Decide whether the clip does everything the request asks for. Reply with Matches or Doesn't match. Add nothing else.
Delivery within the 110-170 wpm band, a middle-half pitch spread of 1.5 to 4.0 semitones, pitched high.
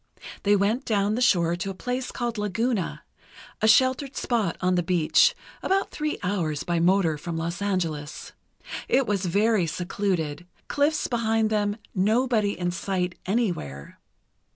Doesn't match